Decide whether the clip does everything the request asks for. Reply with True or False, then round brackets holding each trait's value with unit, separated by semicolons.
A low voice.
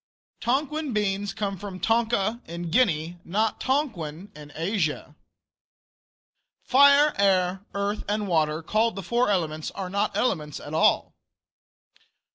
False (200 Hz)